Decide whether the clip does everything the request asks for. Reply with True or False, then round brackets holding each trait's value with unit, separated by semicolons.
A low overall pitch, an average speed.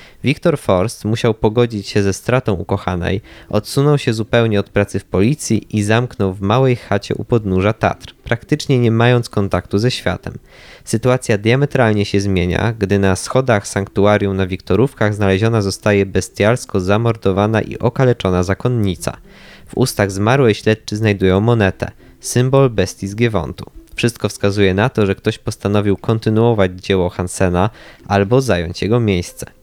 True (105 Hz; 140 wpm)